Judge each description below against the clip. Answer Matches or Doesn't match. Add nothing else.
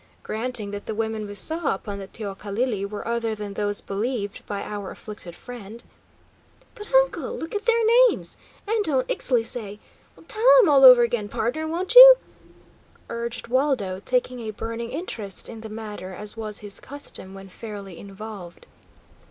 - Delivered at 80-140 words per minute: Doesn't match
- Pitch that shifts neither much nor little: Matches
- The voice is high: Matches